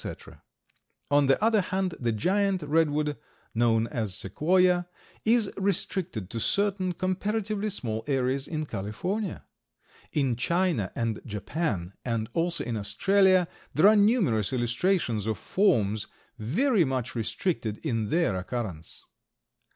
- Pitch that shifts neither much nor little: No, wide, 8.8 semitones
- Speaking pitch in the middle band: Yes, medium, 150 Hz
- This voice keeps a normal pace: No, slow, 120 wpm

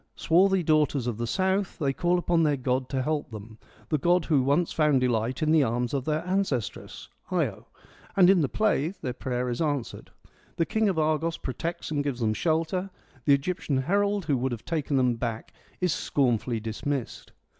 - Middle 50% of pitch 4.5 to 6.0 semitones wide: Yes, average, 5.2 semitones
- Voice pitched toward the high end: No, medium, 145 Hz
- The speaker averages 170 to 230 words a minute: Yes, average, 190 wpm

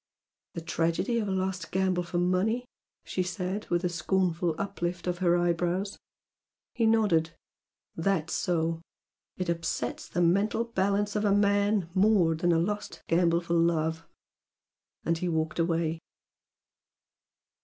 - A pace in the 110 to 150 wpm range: Yes, slow, 135 wpm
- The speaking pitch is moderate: Yes, medium, 180 Hz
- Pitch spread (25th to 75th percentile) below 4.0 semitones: Yes, average, 3.0 semitones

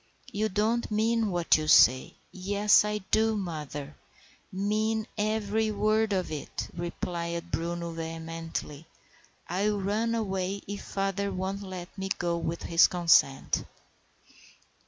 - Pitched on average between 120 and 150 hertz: No, high, 190 Hz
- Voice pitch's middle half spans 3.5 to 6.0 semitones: Yes, average, 3.8 semitones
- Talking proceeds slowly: Yes, slow, 115 wpm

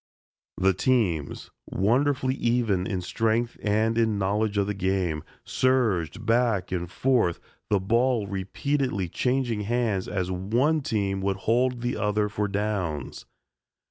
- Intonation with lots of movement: No, average, 4.1 semitones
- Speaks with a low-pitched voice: Yes, low, 105 Hz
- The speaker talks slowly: Yes, slow, 130 wpm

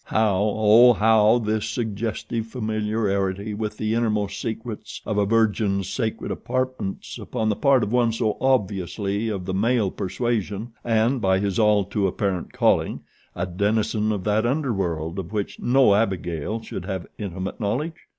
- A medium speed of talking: Yes, average, 150 wpm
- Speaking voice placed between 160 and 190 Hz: No, low, 105 Hz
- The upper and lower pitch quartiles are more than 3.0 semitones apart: No, narrow, 2.6 semitones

